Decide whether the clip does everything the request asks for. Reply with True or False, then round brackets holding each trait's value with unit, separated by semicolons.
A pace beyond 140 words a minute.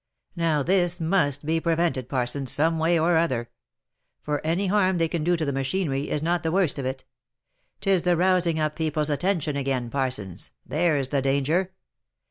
True (175 wpm)